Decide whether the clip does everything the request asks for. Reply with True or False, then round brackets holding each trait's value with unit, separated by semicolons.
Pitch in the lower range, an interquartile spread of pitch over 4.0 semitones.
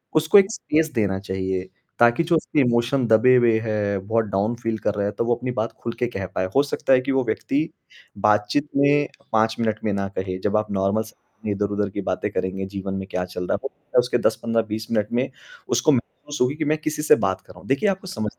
True (110 Hz; 4.6 semitones)